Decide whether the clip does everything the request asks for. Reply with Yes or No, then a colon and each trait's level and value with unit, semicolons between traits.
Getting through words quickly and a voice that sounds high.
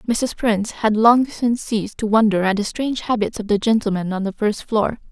Yes: fast, 225 wpm; high, 215 Hz